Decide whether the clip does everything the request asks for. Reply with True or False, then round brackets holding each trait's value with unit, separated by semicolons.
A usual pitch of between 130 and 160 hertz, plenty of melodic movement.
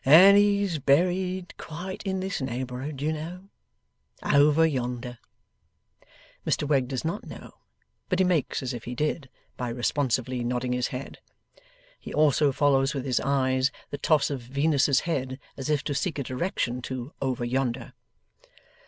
False (140 Hz; 4.0 semitones)